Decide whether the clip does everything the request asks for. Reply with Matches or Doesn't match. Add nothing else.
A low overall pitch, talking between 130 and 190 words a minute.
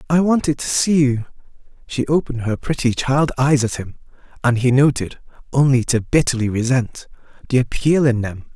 Matches